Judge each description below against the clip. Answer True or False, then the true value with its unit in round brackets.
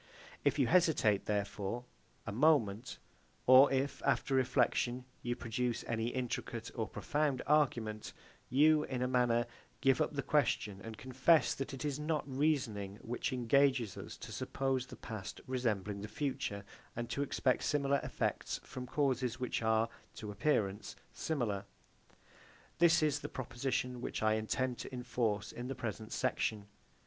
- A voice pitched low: True (125 Hz)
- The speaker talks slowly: False (150 wpm)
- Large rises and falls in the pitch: False (3.8 semitones)